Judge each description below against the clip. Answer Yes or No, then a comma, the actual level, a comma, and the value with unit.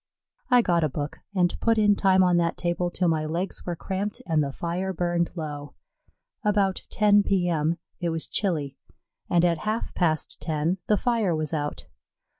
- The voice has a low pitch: No, medium, 175 Hz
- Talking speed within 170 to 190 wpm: Yes, average, 175 wpm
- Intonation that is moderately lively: Yes, average, 3.3 semitones